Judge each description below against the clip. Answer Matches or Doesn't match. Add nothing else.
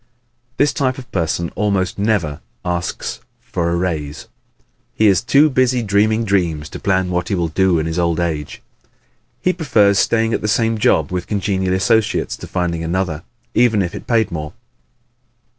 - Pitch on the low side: Matches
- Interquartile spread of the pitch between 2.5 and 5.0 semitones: Matches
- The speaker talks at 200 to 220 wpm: Doesn't match